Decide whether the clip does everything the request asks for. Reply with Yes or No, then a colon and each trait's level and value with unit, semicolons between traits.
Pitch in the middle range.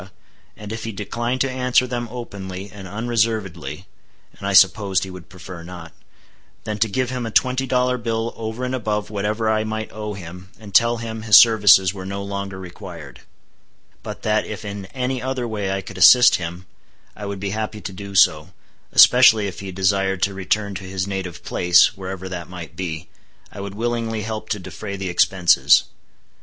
No: low, 100 Hz